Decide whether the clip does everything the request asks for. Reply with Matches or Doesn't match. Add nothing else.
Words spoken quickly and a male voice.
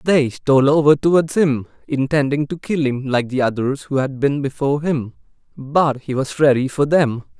Doesn't match